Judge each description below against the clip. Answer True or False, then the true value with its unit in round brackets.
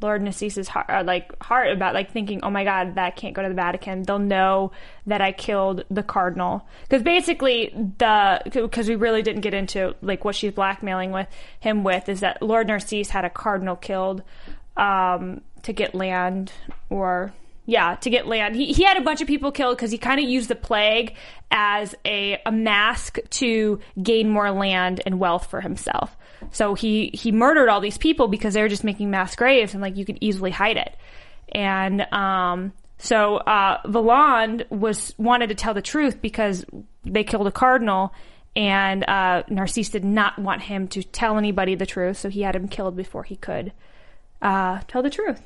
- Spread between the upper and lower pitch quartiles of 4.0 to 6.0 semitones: False (2.8 semitones)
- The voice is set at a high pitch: True (205 Hz)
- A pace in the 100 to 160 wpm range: False (195 wpm)